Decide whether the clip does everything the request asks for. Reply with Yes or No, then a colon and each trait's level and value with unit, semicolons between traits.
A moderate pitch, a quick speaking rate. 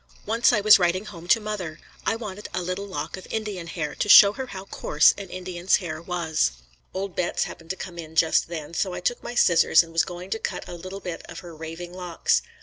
Yes: medium, 180 Hz; fast, 235 wpm